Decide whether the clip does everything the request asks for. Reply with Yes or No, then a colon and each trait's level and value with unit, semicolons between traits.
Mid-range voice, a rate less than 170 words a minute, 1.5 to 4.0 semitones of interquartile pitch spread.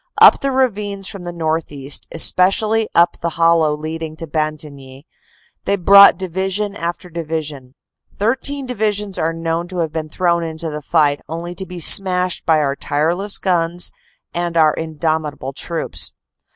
Yes: medium, 170 Hz; average, 155 wpm; average, 3.3 semitones